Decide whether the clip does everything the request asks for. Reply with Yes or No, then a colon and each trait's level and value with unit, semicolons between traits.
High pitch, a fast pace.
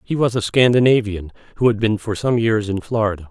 No: low, 110 Hz; fast, 220 wpm